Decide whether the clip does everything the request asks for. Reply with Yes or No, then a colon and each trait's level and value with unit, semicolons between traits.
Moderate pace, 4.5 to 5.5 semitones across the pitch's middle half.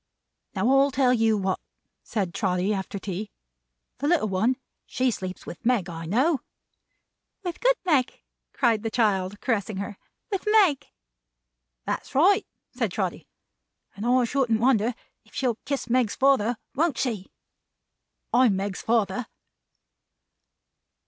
No: slow, 130 wpm; average, 4.9 semitones